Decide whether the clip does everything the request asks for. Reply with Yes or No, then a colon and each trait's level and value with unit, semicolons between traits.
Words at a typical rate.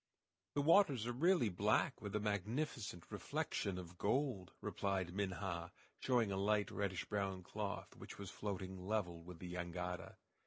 Yes: average, 150 wpm